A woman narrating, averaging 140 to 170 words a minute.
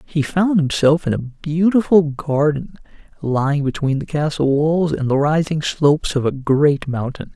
No: male; average, 165 wpm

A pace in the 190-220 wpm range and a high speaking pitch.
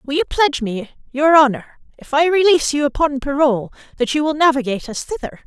Yes: average, 200 wpm; very high, 285 Hz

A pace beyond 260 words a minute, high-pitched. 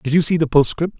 No: fast, 300 wpm; medium, 155 Hz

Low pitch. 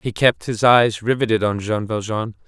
Yes: low, 110 Hz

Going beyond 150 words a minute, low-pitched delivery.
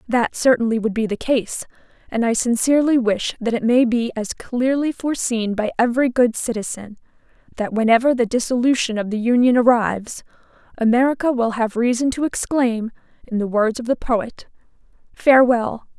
No: average, 160 wpm; high, 240 Hz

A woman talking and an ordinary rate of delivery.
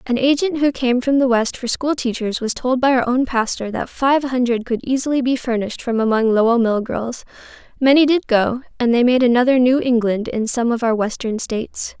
No: female; fast, 215 wpm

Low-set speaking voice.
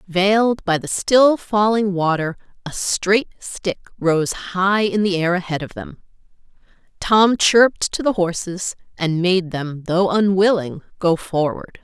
No: high, 190 Hz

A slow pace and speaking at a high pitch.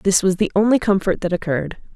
No: fast, 215 wpm; high, 195 Hz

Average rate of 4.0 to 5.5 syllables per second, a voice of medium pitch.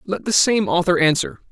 Yes: 5.3 syllables/s; medium, 175 Hz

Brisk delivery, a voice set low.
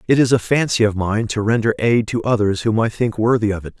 Yes: fast, 270 wpm; low, 110 Hz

